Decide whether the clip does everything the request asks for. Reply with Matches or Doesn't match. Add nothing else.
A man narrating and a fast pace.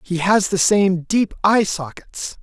Doesn't match